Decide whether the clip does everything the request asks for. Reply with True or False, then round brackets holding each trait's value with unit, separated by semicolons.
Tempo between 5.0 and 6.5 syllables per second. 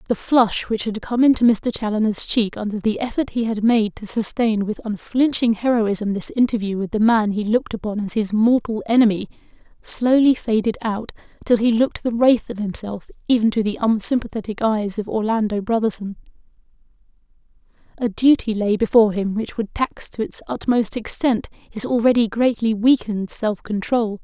True (5.2 syllables/s)